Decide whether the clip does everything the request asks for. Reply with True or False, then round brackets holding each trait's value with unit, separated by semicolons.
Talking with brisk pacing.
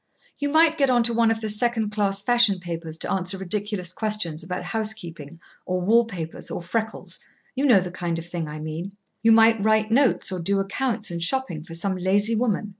True (210 wpm)